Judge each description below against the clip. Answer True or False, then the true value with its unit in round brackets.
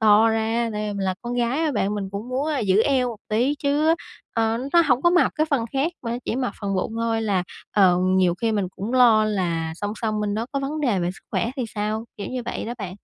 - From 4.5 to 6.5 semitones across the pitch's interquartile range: False (3.7 semitones)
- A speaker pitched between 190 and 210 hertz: False (225 Hz)